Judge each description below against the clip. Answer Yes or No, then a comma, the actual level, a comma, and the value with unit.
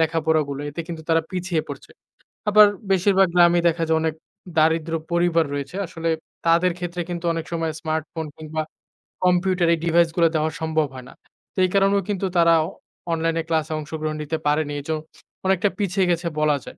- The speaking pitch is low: No, medium, 165 Hz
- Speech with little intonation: Yes, narrow, 2.0 semitones